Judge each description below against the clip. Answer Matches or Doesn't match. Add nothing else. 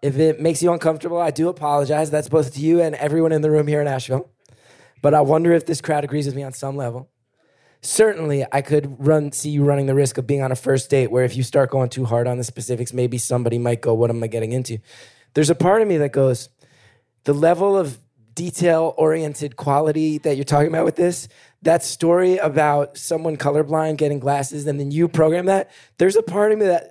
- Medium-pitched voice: Matches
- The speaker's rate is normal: Doesn't match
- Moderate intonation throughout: Matches